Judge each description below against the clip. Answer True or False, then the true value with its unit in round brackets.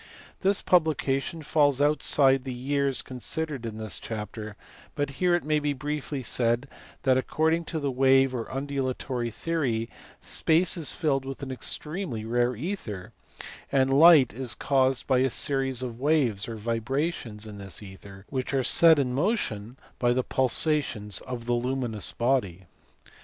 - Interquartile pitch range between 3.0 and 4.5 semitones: True (3.8 semitones)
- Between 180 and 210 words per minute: False (155 wpm)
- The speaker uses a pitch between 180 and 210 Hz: False (130 Hz)